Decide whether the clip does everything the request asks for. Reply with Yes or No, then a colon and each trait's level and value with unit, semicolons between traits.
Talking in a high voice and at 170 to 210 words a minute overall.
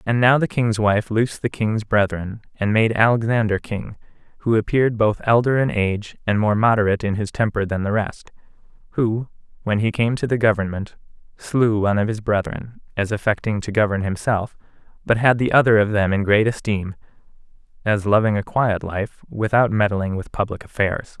No: low, 110 Hz; average, 180 wpm